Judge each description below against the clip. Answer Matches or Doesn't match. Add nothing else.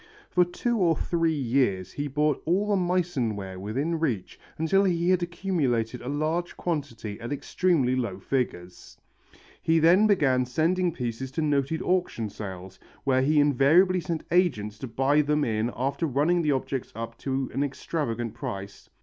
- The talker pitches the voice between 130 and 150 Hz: Matches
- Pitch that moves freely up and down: Matches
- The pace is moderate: Matches